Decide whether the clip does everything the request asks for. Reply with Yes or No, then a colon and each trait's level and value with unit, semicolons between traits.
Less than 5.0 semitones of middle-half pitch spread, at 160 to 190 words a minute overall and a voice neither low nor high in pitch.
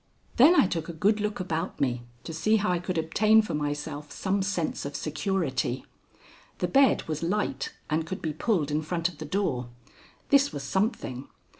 No: average, 5.3 semitones; average, 185 wpm; medium, 165 Hz